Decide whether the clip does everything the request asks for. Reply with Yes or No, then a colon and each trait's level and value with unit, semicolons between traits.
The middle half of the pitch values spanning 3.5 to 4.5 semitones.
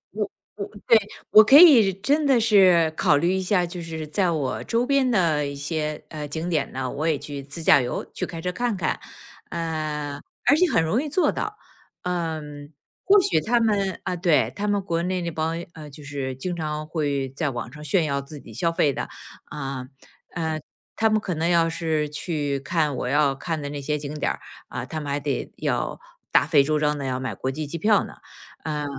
Yes: average, 4.0 semitones